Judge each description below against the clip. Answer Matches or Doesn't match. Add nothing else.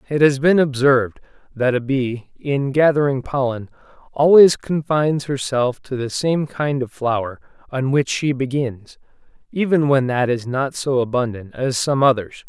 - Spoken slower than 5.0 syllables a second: Matches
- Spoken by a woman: Doesn't match